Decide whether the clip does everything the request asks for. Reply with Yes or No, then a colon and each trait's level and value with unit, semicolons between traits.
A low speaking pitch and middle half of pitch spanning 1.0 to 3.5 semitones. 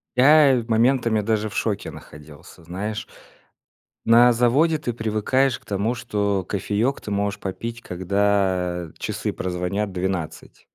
No: low, 105 Hz; average, 4.0 semitones